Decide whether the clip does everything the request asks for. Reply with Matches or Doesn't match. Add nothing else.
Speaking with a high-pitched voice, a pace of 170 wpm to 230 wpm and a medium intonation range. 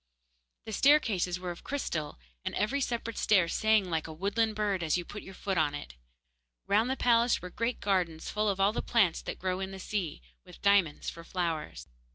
Matches